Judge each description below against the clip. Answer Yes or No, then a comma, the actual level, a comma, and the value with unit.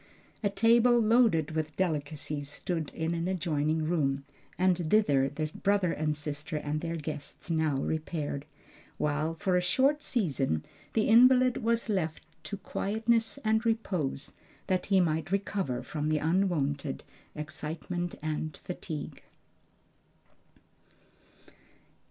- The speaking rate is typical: No, slow, 120 wpm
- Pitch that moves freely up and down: No, average, 4.8 semitones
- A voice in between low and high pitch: Yes, medium, 165 Hz